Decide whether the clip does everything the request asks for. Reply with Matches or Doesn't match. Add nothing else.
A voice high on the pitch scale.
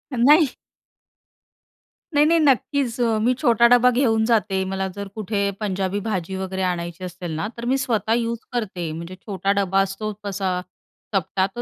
Matches